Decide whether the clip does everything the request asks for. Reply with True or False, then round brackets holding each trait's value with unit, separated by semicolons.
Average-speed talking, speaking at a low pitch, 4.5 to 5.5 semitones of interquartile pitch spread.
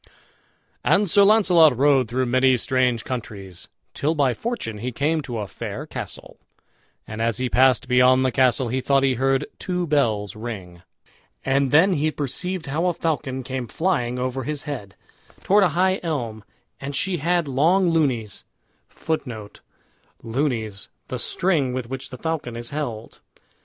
True (155 wpm; 130 Hz; 4.8 semitones)